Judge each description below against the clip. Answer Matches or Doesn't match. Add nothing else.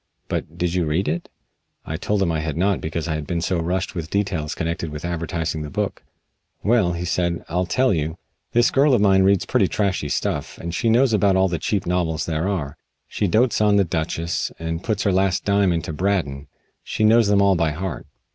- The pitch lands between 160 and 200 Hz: Doesn't match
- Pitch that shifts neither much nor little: Matches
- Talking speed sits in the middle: Doesn't match